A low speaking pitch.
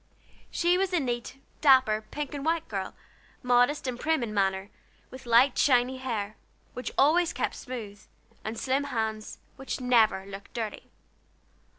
No: very high, 250 Hz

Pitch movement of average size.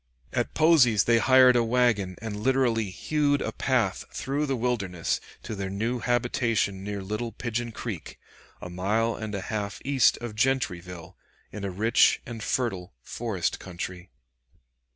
Yes: average, 3.9 semitones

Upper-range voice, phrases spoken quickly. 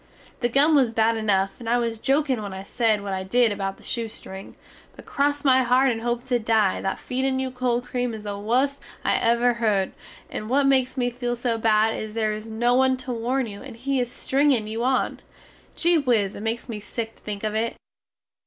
Yes: high, 235 Hz; fast, 220 wpm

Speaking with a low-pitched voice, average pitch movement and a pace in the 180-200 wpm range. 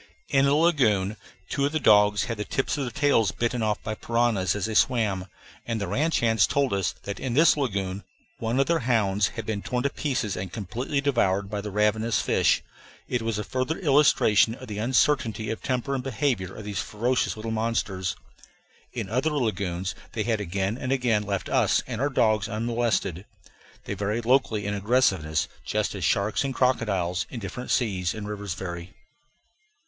Yes: low, 110 Hz; average, 4.1 semitones; average, 185 wpm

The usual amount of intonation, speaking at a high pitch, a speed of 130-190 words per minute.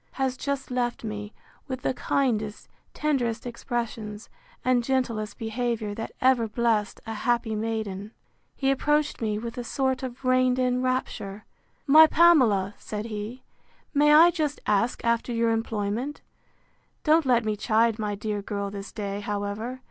Yes: average, 3.4 semitones; high, 235 Hz; average, 150 wpm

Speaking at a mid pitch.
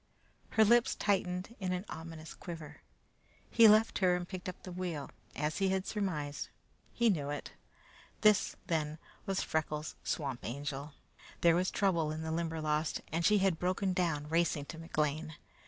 Yes: medium, 170 Hz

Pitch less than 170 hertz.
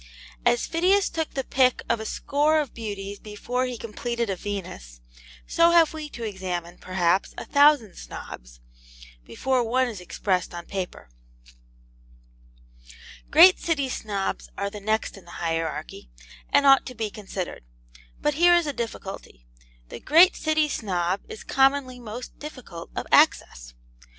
No: high, 230 Hz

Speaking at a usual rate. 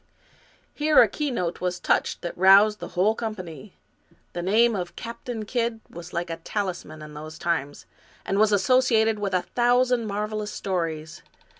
Yes: average, 160 wpm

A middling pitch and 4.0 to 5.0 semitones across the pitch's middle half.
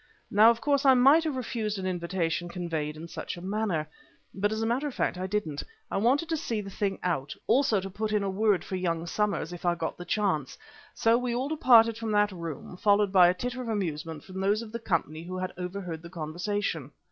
No: high, 195 Hz; average, 4.5 semitones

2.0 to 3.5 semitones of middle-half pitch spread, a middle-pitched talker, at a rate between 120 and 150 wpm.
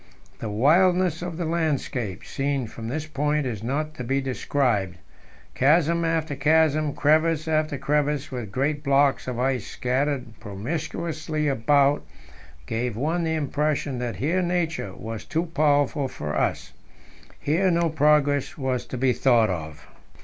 No: average, 3.9 semitones; medium, 145 Hz; average, 140 wpm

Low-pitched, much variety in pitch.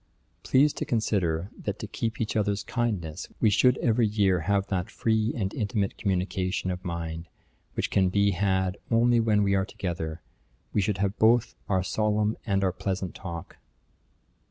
No: low, 100 Hz; average, 2.8 semitones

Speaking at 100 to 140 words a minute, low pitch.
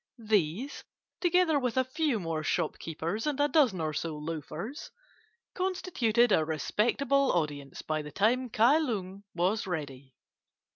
No: slow, 135 wpm; high, 210 Hz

